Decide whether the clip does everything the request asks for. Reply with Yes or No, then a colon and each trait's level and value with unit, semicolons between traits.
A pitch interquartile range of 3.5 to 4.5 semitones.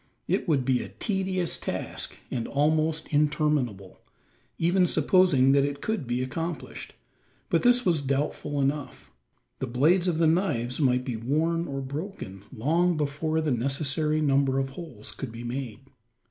Yes: average, 3.9 semitones